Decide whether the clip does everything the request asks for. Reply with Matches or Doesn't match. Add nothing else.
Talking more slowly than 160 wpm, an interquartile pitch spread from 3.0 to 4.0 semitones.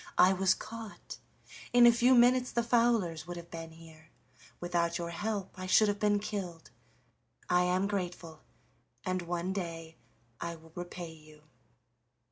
Matches